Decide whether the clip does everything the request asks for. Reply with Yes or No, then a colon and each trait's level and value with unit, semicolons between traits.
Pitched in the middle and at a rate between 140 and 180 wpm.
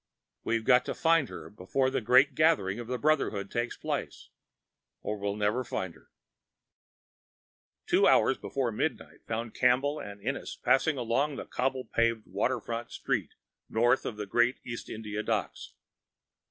No: low, 120 Hz; average, 150 wpm